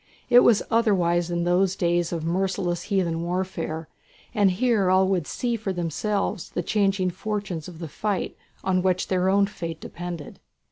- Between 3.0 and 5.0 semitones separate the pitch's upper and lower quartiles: No, narrow, 2.5 semitones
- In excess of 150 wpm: Yes, average, 160 wpm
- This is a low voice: No, medium, 185 Hz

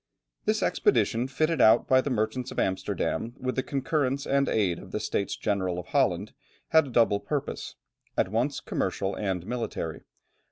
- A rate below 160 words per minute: No, average, 165 wpm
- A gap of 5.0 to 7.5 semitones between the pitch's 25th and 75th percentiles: Yes, average, 5.3 semitones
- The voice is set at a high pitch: No, low, 120 Hz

